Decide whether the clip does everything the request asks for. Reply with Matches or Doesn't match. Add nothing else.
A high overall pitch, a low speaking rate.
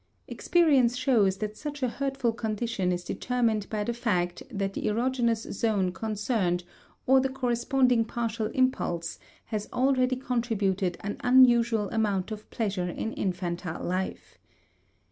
Matches